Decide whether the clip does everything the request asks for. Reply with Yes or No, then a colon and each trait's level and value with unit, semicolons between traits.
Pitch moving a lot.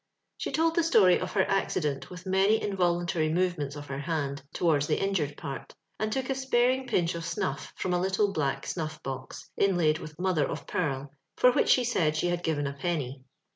No: average, 4.9 semitones